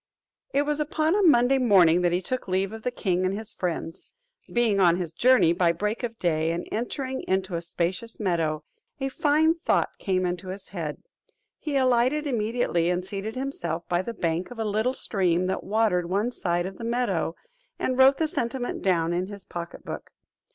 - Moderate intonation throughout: No, wide, 5.8 semitones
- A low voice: No, high, 200 Hz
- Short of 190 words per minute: No, average, 195 wpm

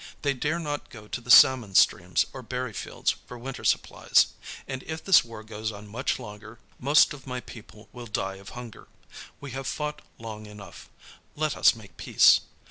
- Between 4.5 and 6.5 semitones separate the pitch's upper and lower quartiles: No, average, 3.8 semitones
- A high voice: No, low, 120 Hz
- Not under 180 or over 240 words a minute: Yes, average, 185 wpm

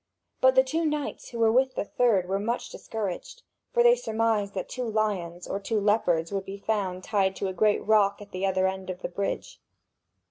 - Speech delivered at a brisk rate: Yes, fast, 210 wpm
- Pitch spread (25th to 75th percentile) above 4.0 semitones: No, average, 3.3 semitones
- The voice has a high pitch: Yes, high, 205 Hz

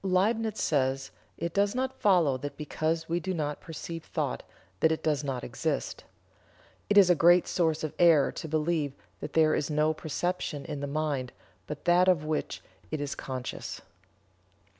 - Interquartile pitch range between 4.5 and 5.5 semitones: No, average, 3.3 semitones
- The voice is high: No, medium, 155 Hz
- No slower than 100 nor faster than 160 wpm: No, average, 170 wpm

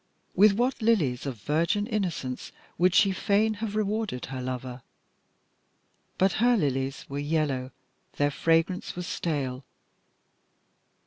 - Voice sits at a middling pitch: Yes, medium, 165 Hz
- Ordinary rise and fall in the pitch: No, wide, 7.6 semitones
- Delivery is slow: Yes, slow, 120 wpm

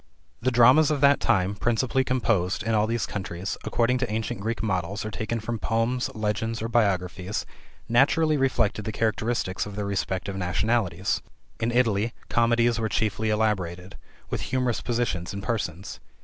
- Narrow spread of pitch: No, average, 3.1 semitones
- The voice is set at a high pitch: No, low, 110 Hz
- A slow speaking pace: No, average, 155 wpm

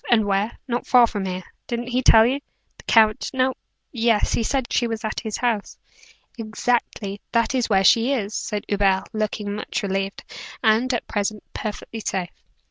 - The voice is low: No, high, 220 Hz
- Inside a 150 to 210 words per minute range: Yes, average, 175 wpm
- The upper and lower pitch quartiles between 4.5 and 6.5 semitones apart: No, average, 2.9 semitones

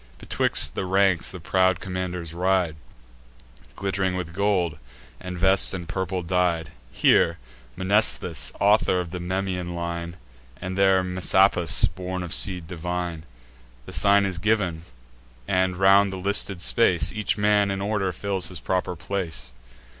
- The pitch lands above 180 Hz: No, very low, 95 Hz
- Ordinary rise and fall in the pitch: No, narrow, 1.9 semitones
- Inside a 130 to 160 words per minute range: Yes, average, 140 wpm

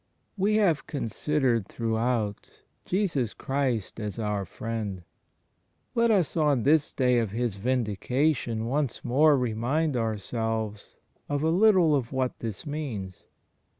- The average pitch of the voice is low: Yes, low, 125 Hz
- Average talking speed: No, slow, 120 wpm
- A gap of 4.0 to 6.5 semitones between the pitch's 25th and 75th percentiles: Yes, average, 5.2 semitones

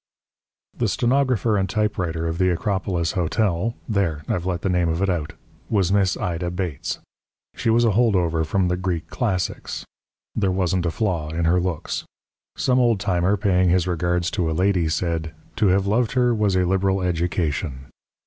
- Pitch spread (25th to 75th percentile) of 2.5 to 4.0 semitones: Yes, average, 2.9 semitones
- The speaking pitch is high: No, very low, 90 Hz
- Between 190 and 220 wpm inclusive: No, average, 175 wpm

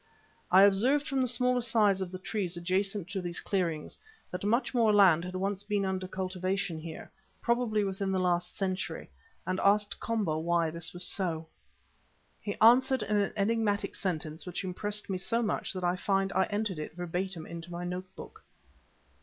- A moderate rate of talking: Yes, average, 175 wpm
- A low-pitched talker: No, high, 190 Hz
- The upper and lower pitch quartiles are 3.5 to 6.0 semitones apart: No, average, 2.8 semitones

